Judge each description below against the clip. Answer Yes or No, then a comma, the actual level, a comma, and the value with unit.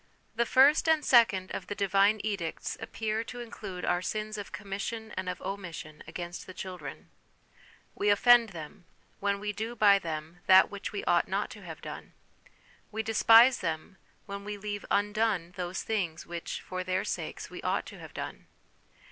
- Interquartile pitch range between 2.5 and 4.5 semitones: Yes, average, 3.2 semitones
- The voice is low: No, high, 200 Hz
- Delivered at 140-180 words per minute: Yes, average, 175 wpm